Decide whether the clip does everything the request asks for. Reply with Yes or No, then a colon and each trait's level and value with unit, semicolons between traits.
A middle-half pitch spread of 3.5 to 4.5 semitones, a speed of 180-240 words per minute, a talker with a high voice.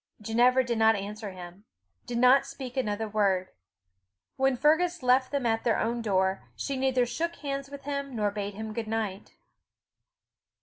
No: average, 4.2 semitones; average, 165 wpm; high, 235 Hz